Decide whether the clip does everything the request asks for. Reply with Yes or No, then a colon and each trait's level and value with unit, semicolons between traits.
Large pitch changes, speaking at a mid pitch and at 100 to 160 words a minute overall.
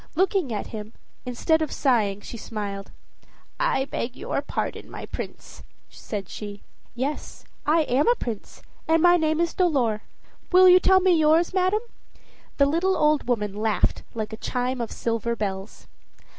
No: wide, 7.6 semitones; very high, 265 Hz; average, 155 wpm